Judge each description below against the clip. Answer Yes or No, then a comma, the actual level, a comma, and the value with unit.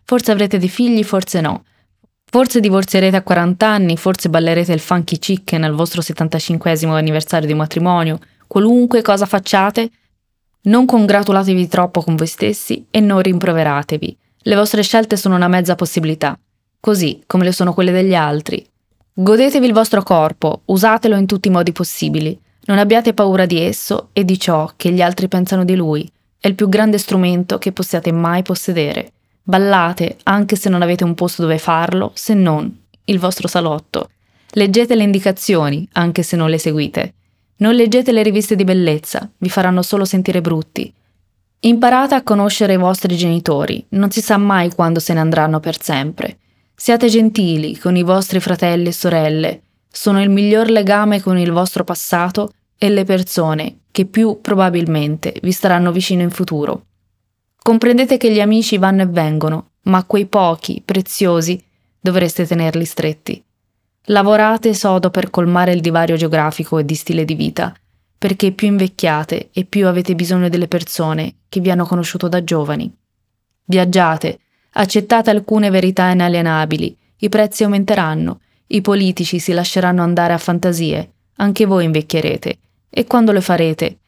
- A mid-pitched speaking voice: Yes, medium, 180 Hz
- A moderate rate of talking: Yes, average, 155 wpm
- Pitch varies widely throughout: No, average, 3.5 semitones